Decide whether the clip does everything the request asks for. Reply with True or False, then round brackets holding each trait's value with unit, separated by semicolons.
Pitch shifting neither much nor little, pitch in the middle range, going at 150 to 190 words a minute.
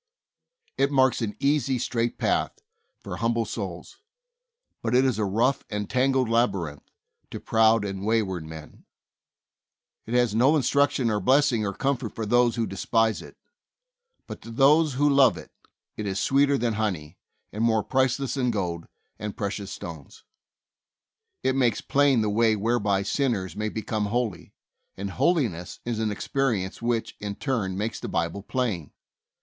False (4.3 semitones; 115 Hz; 160 wpm)